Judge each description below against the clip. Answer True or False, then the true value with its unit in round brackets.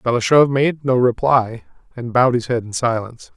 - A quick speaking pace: False (180 wpm)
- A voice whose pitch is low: True (125 Hz)